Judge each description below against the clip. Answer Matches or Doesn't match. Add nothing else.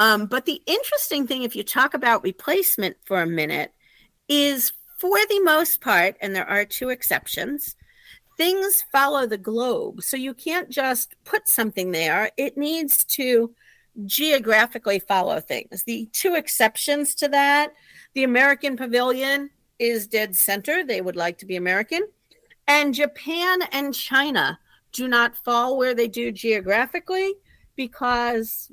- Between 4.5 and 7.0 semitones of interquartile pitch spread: Matches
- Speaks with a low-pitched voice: Doesn't match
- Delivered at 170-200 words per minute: Doesn't match